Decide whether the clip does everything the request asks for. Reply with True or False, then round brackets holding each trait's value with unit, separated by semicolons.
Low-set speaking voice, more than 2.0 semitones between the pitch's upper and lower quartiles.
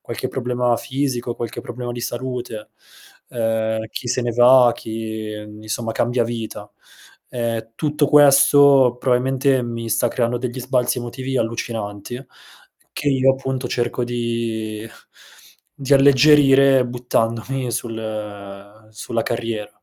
True (120 Hz; 2.6 semitones)